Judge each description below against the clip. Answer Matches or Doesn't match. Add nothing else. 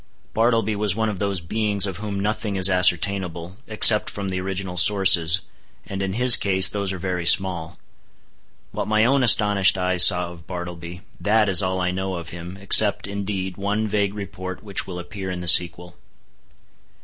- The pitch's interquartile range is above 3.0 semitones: Doesn't match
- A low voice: Matches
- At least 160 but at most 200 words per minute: Matches